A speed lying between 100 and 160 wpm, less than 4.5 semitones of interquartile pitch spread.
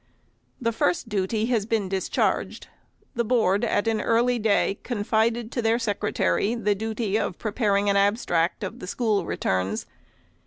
Yes: average, 150 wpm; narrow, 2.4 semitones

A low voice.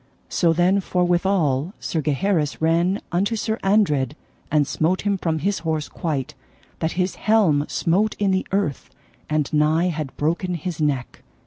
No: medium, 170 Hz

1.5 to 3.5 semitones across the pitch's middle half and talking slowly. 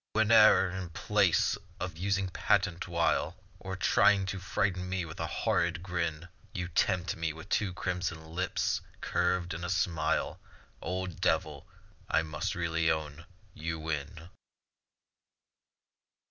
Yes: narrow, 2.4 semitones; slow, 125 wpm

